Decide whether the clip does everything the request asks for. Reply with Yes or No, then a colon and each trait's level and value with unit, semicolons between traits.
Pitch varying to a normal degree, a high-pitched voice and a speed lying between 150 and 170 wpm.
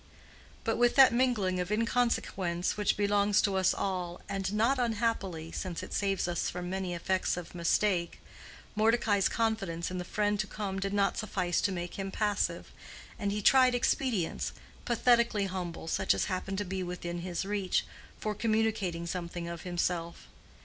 Yes: average, 3.2 semitones; high, 195 Hz; average, 165 wpm